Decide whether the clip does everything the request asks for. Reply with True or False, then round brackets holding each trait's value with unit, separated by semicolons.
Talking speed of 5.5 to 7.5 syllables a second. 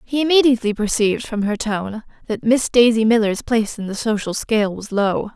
True (5.6 syllables/s)